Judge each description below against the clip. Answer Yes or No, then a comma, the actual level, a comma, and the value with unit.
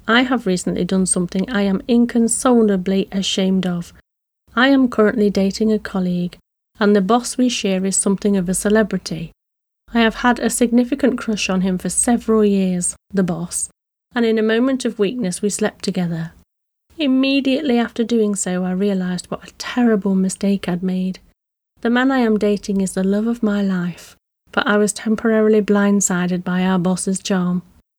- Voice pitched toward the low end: No, high, 205 Hz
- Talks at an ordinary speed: Yes, average, 170 wpm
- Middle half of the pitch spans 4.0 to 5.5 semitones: No, average, 3.5 semitones